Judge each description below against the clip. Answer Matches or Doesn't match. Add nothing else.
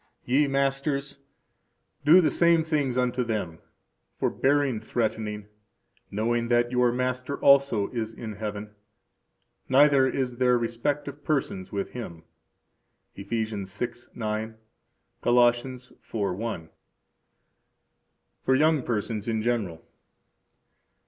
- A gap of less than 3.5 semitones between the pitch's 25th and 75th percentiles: Doesn't match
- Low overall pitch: Matches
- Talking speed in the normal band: Doesn't match